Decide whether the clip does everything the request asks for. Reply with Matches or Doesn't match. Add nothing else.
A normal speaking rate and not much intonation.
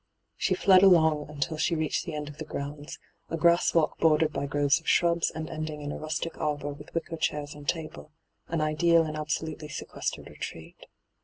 Matches